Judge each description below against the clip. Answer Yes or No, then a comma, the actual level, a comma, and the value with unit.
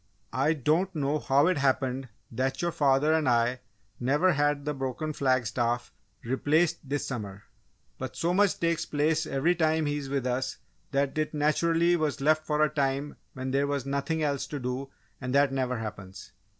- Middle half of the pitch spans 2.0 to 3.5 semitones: Yes, average, 3.0 semitones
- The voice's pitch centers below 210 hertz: Yes, medium, 140 Hz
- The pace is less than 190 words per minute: Yes, average, 180 wpm